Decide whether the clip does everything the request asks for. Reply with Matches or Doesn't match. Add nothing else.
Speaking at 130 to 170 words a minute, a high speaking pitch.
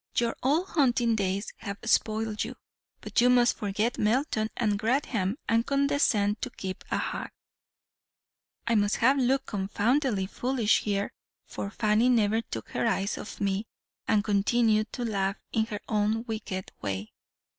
Matches